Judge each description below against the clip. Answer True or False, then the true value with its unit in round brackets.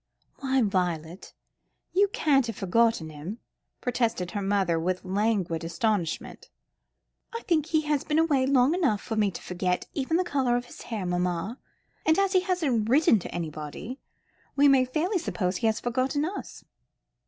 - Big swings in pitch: True (7.9 semitones)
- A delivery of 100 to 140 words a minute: False (165 wpm)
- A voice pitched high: True (230 Hz)